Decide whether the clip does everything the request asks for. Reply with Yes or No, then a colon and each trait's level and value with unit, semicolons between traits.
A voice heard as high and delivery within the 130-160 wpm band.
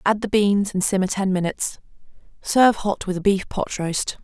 No: high, 195 Hz; average, 200 wpm